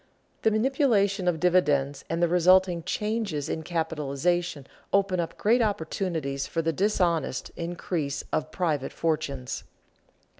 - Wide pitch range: No, average, 3.7 semitones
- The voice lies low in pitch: No, medium, 170 Hz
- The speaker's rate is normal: No, slow, 120 wpm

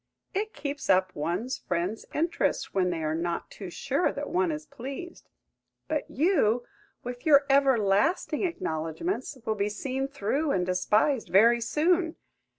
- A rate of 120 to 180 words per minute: Yes, average, 145 wpm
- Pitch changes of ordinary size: No, wide, 7.6 semitones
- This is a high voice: Yes, very high, 255 Hz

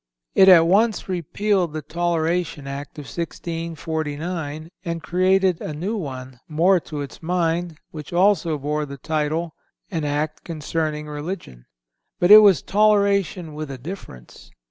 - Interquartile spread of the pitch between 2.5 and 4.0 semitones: Yes, average, 3.2 semitones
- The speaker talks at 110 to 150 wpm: Yes, average, 140 wpm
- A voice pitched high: No, medium, 165 Hz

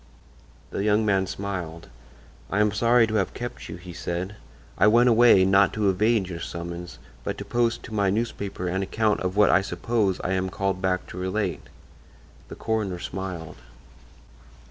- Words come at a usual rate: Yes, average, 170 wpm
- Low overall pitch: Yes, very low, 95 Hz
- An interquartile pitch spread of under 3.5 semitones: Yes, average, 2.8 semitones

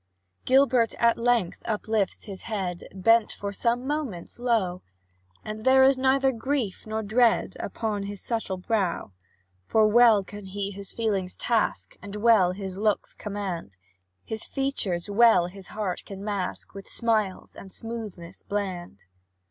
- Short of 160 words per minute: Yes, average, 140 wpm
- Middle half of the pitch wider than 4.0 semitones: No, average, 3.4 semitones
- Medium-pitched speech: No, high, 210 Hz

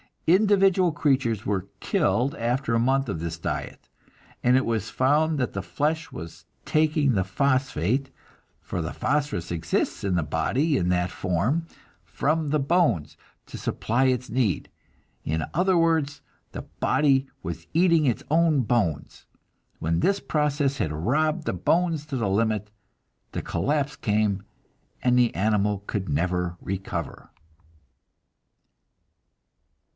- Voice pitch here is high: No, low, 125 Hz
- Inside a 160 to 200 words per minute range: No, slow, 135 wpm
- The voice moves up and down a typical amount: No, wide, 7.7 semitones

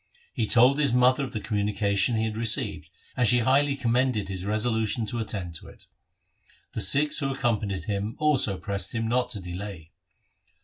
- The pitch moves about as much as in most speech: Yes, average, 3.7 semitones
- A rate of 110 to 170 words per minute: No, average, 185 wpm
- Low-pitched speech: Yes, low, 115 Hz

